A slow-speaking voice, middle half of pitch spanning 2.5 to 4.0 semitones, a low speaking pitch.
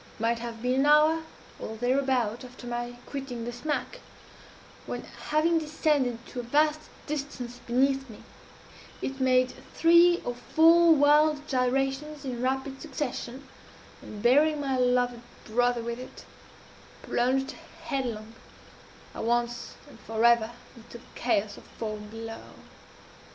No: slow, 130 wpm; average, 3.3 semitones; very high, 255 Hz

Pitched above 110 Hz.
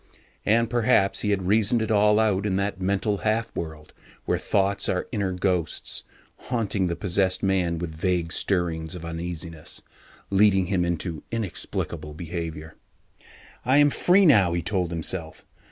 No: very low, 95 Hz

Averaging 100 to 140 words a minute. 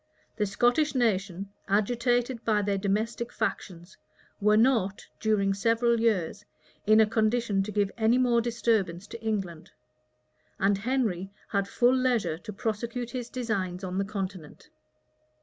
Yes: slow, 135 wpm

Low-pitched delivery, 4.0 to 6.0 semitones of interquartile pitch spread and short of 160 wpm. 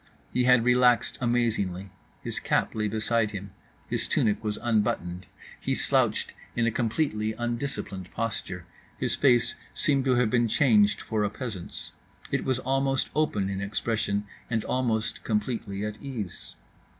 No: low, 110 Hz; average, 3.1 semitones; average, 140 wpm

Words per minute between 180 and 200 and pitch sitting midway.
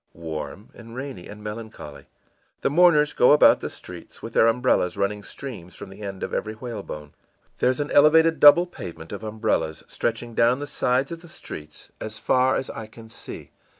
No: average, 185 wpm; low, 115 Hz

